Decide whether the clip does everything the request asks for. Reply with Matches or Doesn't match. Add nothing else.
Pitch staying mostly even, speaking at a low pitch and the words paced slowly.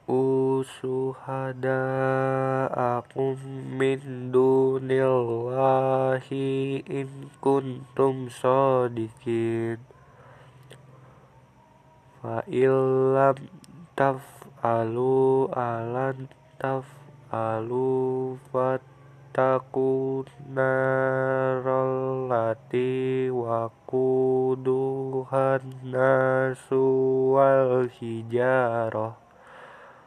Matches